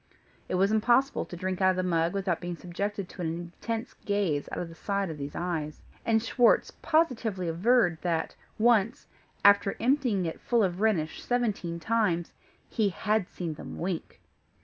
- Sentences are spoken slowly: No, average, 170 wpm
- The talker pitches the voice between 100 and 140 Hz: No, high, 195 Hz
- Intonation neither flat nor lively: Yes, average, 4.4 semitones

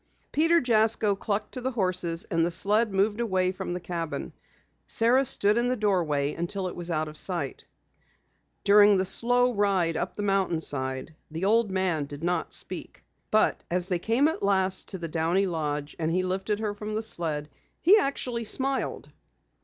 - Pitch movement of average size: Yes, average, 4.4 semitones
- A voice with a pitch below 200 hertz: Yes, high, 190 Hz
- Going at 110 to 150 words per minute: No, average, 180 wpm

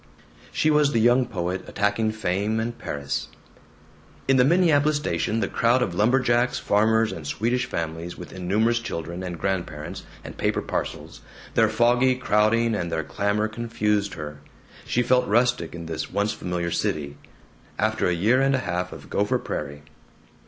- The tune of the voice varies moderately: No, wide, 5.7 semitones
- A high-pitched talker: No, low, 105 Hz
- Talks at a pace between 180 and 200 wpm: No, average, 160 wpm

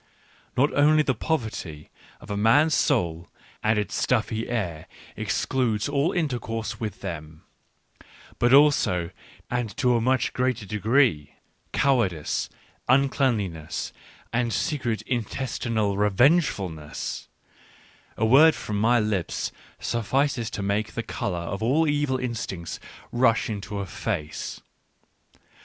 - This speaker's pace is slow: Yes, slow, 115 wpm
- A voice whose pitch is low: Yes, low, 115 Hz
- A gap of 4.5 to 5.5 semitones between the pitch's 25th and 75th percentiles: Yes, average, 4.8 semitones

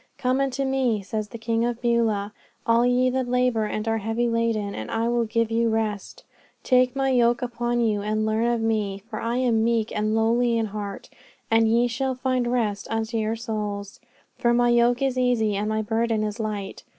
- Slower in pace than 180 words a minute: No, average, 200 wpm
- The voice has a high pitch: Yes, high, 230 Hz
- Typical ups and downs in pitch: No, narrow, 1.9 semitones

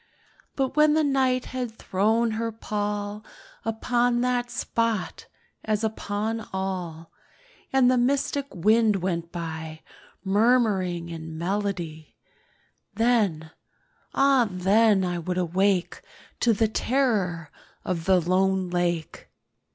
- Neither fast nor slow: No, slow, 105 wpm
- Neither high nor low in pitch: No, high, 205 Hz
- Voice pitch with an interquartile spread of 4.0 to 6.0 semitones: Yes, average, 5.1 semitones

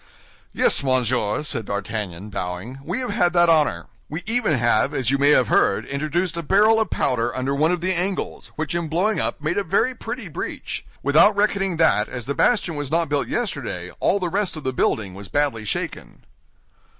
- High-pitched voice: No, medium, 150 Hz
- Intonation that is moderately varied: No, wide, 7.0 semitones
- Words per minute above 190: Yes, average, 200 wpm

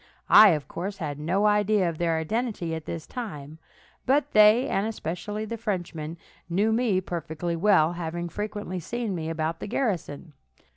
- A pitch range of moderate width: Yes, average, 4.6 semitones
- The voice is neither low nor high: Yes, medium, 180 Hz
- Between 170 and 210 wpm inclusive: No, average, 160 wpm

